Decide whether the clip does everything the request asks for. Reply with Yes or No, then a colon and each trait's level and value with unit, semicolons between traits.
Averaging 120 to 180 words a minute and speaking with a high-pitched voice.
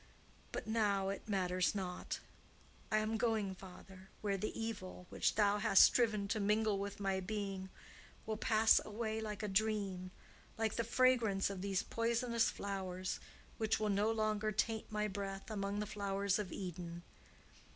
Yes: average, 155 wpm; high, 205 Hz